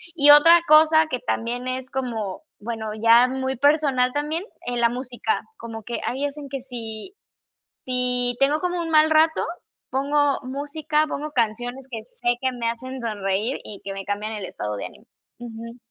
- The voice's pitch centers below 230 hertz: No, very high, 250 Hz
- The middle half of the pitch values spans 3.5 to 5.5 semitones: Yes, average, 3.9 semitones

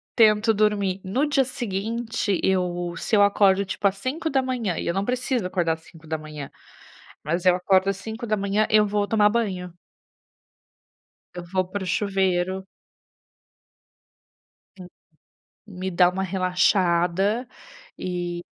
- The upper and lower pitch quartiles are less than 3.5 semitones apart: Yes, average, 3.0 semitones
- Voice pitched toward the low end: No, high, 195 Hz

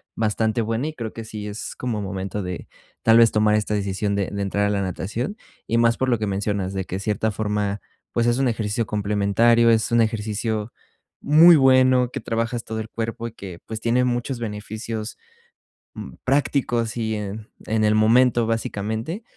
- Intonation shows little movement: Yes, narrow, 2.2 semitones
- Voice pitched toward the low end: Yes, low, 110 Hz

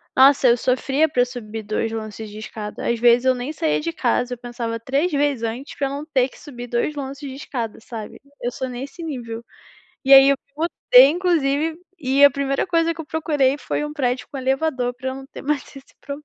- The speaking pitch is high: Yes, very high, 265 Hz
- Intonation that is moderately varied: Yes, average, 3.1 semitones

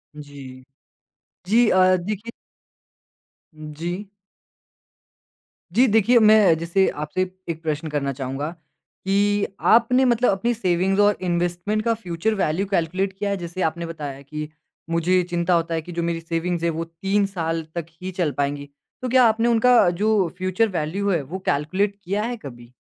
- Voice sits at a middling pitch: Yes, medium, 180 Hz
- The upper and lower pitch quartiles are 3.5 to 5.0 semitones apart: Yes, average, 4.1 semitones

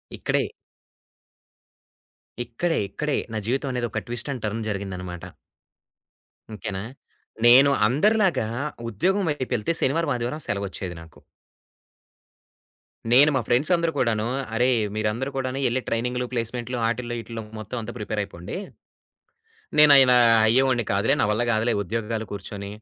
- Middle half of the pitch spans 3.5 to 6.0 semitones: Yes, average, 3.8 semitones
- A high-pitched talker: No, low, 120 Hz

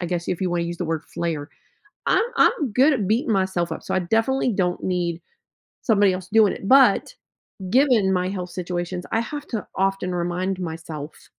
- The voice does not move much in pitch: No, average, 4.0 semitones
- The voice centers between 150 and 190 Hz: Yes, medium, 185 Hz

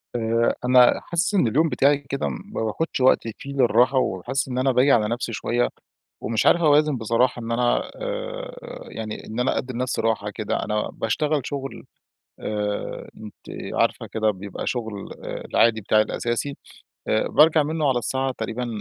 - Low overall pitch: Yes, low, 125 Hz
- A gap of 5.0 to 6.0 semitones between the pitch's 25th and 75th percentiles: No, average, 4.4 semitones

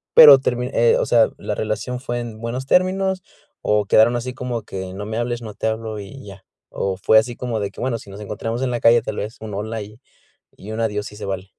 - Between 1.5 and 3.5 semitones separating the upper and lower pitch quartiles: Yes, narrow, 2.6 semitones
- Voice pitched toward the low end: Yes, low, 110 Hz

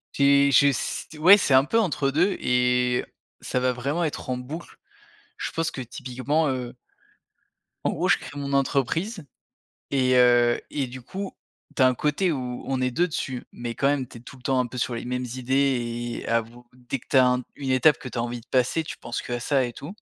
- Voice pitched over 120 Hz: Yes, low, 130 Hz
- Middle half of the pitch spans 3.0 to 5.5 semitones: No, narrow, 2.6 semitones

